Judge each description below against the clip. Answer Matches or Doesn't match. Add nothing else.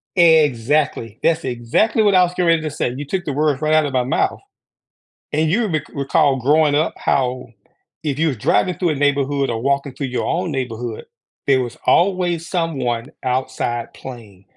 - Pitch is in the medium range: Matches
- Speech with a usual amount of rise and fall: Matches